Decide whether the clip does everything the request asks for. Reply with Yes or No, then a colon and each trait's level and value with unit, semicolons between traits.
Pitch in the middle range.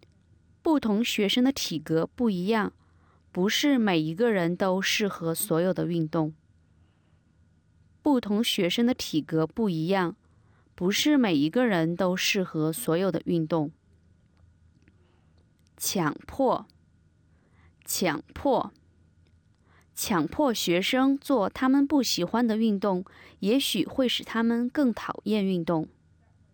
Yes: medium, 170 Hz